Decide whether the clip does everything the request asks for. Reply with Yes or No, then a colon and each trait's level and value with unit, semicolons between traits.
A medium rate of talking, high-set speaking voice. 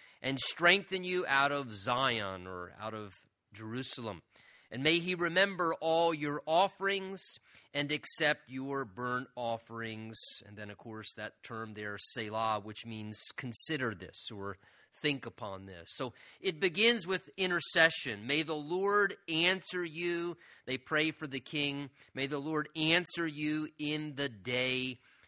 No: average, 145 wpm; medium, 140 Hz